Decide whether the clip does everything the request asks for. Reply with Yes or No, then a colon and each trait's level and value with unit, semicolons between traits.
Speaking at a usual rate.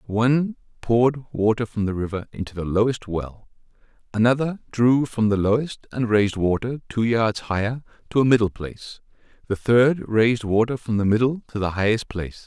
Yes: average, 175 wpm